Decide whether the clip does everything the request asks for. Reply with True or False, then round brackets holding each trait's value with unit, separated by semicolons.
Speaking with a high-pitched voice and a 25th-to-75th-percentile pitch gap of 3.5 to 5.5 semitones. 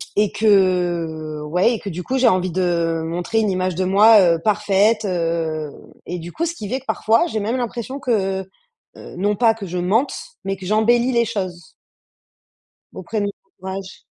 True (195 Hz; 4.0 semitones)